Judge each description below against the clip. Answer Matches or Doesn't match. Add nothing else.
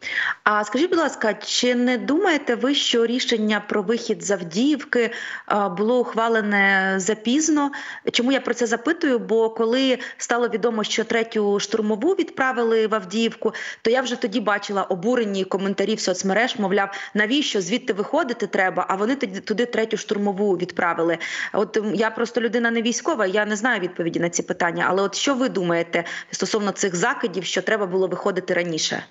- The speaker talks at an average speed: Doesn't match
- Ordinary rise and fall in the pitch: Matches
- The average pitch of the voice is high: Matches